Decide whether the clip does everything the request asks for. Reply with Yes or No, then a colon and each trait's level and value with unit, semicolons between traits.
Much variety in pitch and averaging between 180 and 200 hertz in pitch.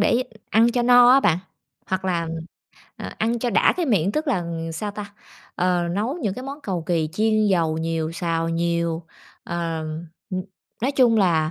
Yes: wide, 5.7 semitones; high, 190 Hz